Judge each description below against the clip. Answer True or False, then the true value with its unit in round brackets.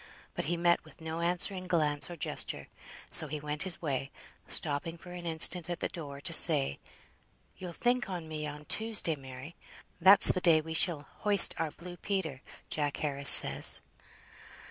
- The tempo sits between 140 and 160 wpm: False (170 wpm)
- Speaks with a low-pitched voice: False (165 Hz)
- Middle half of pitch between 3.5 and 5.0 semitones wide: False (3.1 semitones)